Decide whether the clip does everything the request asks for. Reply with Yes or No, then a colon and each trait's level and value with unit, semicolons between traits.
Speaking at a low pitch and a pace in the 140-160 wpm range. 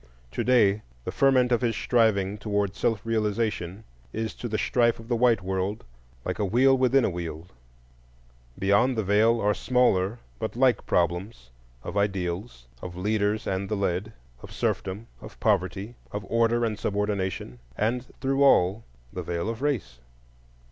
Yes: low, 105 Hz; average, 155 wpm